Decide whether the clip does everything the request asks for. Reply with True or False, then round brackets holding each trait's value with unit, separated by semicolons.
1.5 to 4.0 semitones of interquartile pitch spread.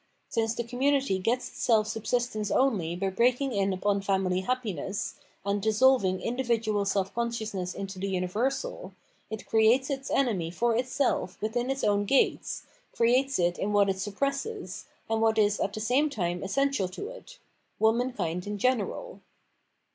False (4.5 semitones)